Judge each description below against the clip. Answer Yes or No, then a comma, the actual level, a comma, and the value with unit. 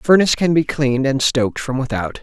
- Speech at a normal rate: No, fast, 240 wpm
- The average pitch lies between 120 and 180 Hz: Yes, low, 135 Hz